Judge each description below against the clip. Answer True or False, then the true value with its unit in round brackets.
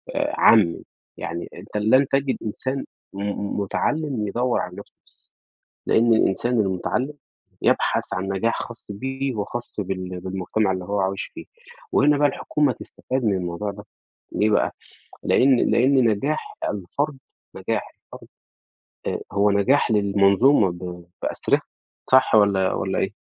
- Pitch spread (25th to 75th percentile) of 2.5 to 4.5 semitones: False (5.2 semitones)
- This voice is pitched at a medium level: False (105 Hz)